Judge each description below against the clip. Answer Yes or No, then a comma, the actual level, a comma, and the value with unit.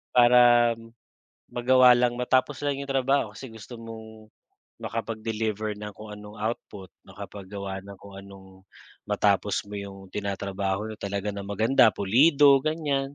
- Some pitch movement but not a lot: Yes, average, 3.7 semitones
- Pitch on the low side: Yes, low, 110 Hz